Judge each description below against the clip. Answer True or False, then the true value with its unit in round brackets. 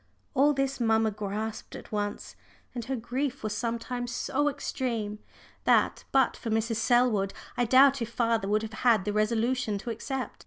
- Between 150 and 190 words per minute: True (165 wpm)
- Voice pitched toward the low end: False (230 Hz)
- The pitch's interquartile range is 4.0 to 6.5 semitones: False (3.0 semitones)